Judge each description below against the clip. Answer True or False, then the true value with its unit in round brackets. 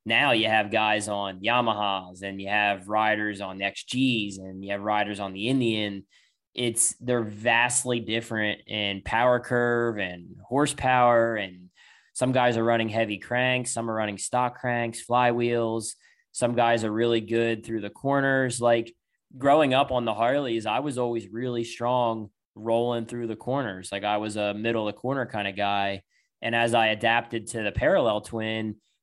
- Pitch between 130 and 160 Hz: False (115 Hz)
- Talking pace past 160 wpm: True (175 wpm)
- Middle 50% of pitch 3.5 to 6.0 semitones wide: False (2.4 semitones)